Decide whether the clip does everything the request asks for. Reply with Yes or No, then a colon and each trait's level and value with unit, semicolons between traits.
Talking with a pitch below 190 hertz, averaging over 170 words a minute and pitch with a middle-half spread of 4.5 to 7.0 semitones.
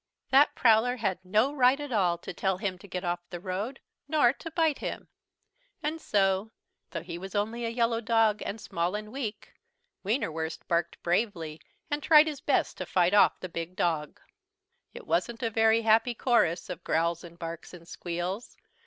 No: high, 205 Hz; average, 180 wpm; average, 5.2 semitones